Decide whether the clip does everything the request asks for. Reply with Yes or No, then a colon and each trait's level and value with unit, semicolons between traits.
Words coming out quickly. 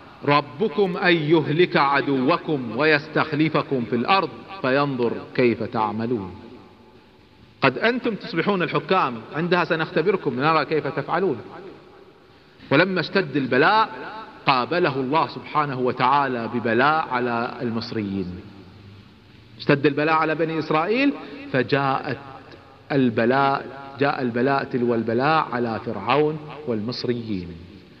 No: average, 90 wpm